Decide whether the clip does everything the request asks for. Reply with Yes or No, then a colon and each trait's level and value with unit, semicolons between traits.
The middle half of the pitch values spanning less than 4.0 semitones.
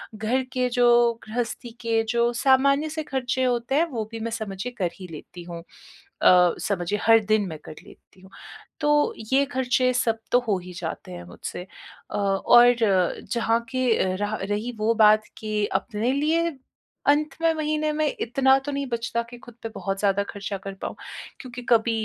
No: average, 4.3 semitones